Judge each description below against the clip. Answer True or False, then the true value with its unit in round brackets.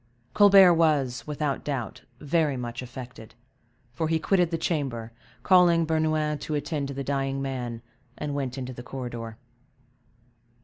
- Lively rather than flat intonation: False (4.1 semitones)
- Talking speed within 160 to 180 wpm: False (140 wpm)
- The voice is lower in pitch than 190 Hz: True (140 Hz)